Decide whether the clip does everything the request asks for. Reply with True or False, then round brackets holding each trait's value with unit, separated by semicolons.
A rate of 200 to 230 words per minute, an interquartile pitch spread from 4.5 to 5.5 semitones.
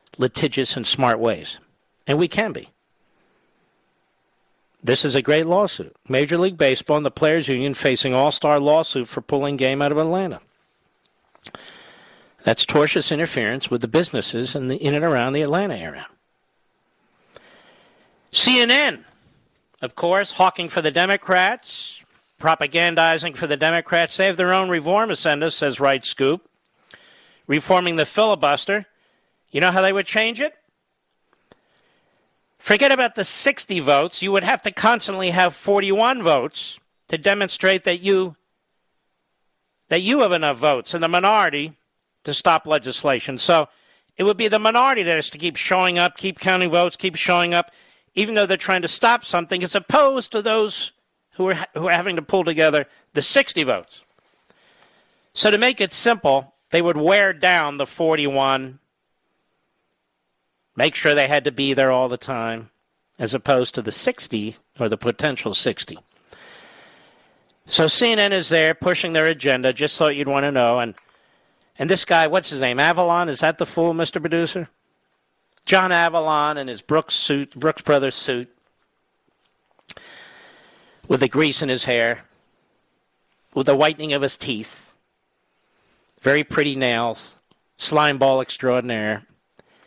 False (150 wpm; 5.1 semitones)